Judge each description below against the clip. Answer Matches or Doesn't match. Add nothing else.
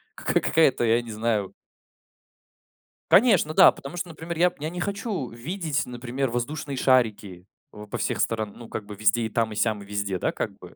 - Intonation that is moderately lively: Doesn't match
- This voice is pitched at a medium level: Doesn't match